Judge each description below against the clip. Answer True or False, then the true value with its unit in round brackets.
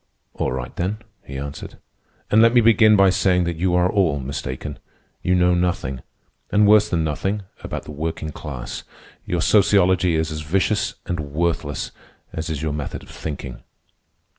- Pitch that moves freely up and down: False (4.7 semitones)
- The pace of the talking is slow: False (165 wpm)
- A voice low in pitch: True (85 Hz)